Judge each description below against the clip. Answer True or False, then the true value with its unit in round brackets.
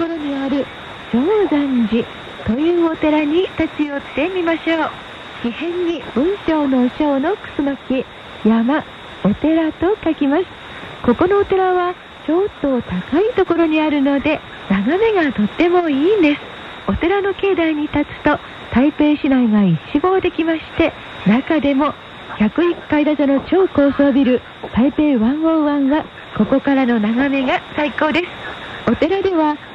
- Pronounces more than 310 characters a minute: False (265 characters per minute)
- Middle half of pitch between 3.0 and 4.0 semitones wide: True (3.5 semitones)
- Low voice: False (300 Hz)